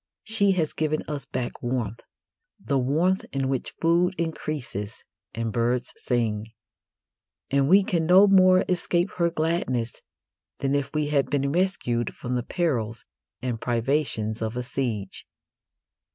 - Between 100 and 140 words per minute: Yes, slow, 135 wpm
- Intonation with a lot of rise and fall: Yes, wide, 6.0 semitones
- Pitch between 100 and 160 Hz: Yes, medium, 140 Hz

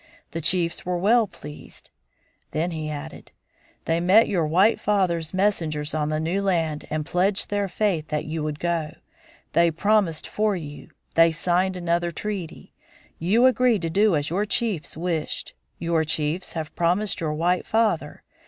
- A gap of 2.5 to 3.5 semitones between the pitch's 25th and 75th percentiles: No, average, 3.9 semitones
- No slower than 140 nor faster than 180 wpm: Yes, average, 160 wpm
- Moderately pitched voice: Yes, medium, 170 Hz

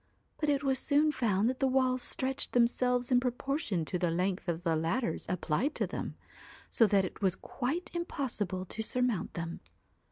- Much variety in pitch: Yes, wide, 6.2 semitones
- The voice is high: Yes, high, 245 Hz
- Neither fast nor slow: Yes, average, 180 wpm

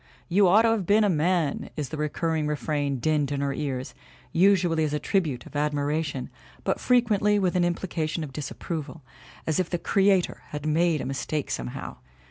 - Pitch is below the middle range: No, medium, 155 Hz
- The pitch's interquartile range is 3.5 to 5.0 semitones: Yes, average, 3.9 semitones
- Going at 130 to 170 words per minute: No, average, 185 wpm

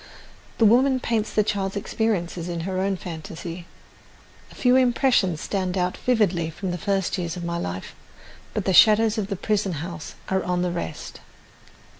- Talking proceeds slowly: No, average, 170 wpm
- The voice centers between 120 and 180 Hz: No, high, 190 Hz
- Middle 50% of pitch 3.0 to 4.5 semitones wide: Yes, average, 3.6 semitones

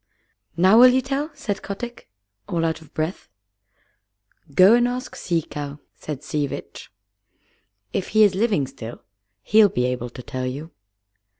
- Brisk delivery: No, average, 155 wpm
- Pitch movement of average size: No, wide, 7.5 semitones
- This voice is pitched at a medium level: Yes, medium, 175 Hz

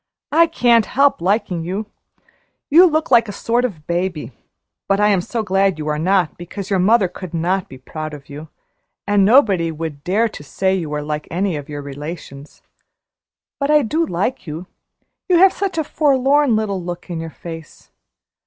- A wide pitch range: Yes, wide, 6.2 semitones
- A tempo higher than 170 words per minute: Yes, average, 185 wpm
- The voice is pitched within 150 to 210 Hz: Yes, high, 190 Hz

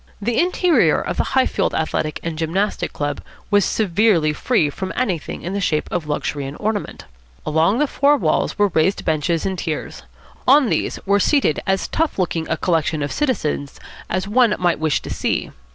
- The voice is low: No, medium, 185 Hz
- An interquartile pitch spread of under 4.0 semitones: No, wide, 5.6 semitones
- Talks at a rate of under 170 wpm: No, average, 180 wpm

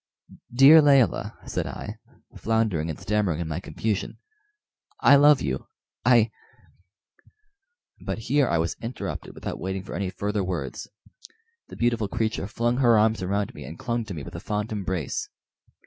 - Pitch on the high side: No, low, 105 Hz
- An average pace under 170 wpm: Yes, average, 160 wpm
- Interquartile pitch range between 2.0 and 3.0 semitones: No, average, 4.5 semitones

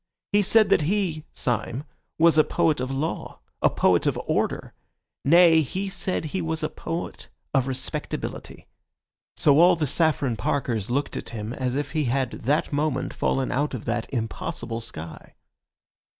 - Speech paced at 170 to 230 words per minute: No, average, 155 wpm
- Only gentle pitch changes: No, average, 4.5 semitones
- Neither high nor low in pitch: Yes, medium, 145 Hz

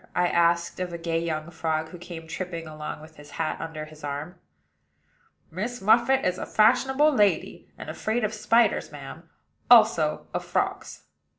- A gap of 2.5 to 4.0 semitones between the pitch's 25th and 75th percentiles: No, average, 5.0 semitones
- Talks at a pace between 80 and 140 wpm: No, average, 165 wpm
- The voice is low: No, medium, 170 Hz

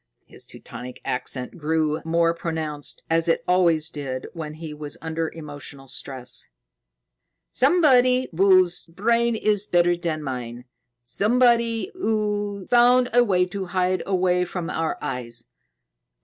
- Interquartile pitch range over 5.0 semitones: Yes, wide, 5.4 semitones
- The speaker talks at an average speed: No, slow, 125 wpm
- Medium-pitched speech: Yes, medium, 175 Hz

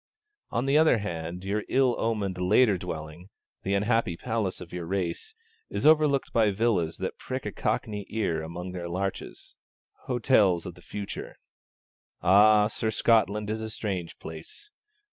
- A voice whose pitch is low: Yes, low, 100 Hz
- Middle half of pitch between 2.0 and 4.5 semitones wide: Yes, average, 4.1 semitones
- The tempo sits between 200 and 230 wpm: No, average, 150 wpm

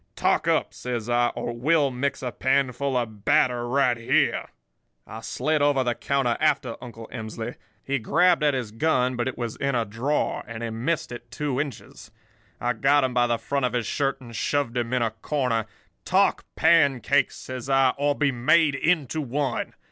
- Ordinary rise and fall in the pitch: Yes, average, 3.0 semitones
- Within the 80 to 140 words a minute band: No, average, 185 wpm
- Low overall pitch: Yes, low, 130 Hz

